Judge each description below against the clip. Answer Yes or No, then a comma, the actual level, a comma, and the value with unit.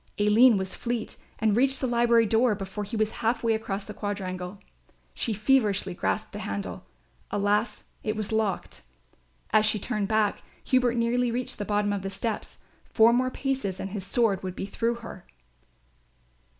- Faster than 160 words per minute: Yes, average, 170 wpm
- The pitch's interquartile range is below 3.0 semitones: Yes, narrow, 2.6 semitones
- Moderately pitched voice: No, high, 215 Hz